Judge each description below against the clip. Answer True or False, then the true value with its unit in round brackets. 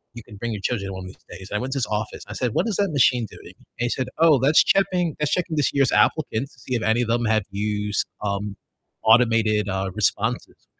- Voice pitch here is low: True (115 Hz)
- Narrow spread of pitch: False (4.8 semitones)